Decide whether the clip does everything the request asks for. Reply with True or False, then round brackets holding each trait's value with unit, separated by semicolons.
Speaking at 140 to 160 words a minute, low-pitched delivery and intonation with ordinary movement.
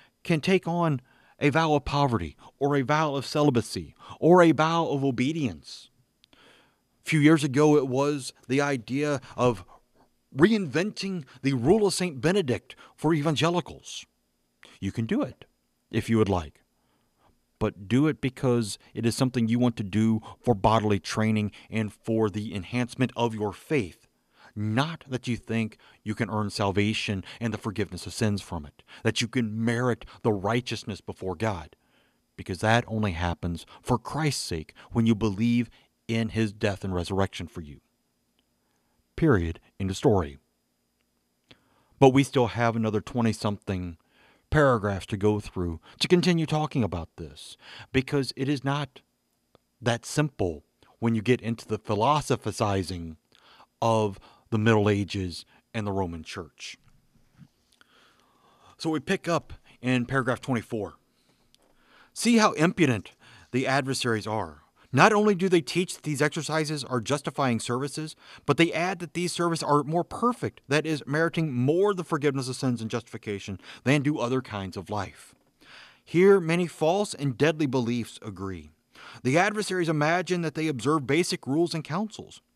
False (150 wpm; 120 Hz; 6.2 semitones)